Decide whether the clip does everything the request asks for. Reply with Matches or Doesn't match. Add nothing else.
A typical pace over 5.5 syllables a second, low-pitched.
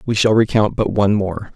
Matches